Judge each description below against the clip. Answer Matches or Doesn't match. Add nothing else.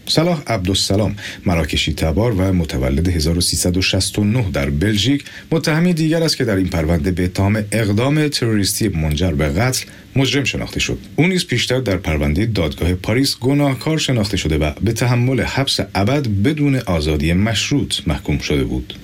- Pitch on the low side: Matches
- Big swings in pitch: Matches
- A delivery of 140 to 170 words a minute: Matches